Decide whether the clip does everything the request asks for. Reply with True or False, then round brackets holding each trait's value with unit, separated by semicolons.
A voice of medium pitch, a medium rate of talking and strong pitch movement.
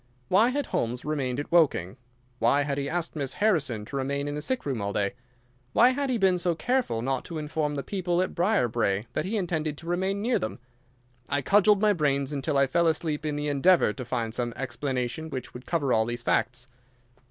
False (145 Hz; 210 wpm; 5.8 semitones)